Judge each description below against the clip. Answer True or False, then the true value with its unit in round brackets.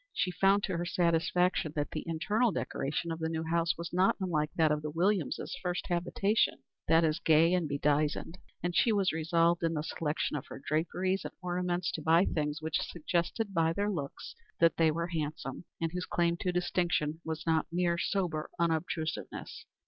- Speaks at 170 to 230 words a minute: True (185 wpm)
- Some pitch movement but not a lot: False (2.1 semitones)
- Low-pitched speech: False (170 Hz)